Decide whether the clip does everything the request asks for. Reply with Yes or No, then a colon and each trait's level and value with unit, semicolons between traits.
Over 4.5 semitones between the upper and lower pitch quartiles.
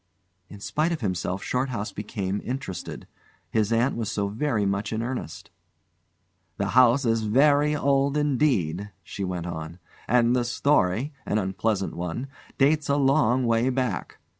Yes: wide, 5.5 semitones